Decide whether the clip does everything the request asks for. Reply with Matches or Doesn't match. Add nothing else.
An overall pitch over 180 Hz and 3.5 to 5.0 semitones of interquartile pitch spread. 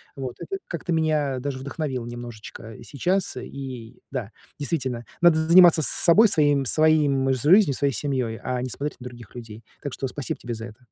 Doesn't match